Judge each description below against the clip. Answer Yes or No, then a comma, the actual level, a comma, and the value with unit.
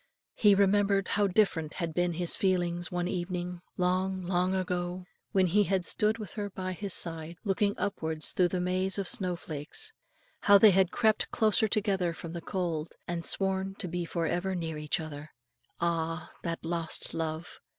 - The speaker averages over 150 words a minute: Yes, average, 175 wpm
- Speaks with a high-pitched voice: No, medium, 180 Hz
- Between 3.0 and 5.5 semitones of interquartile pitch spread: No, narrow, 2.5 semitones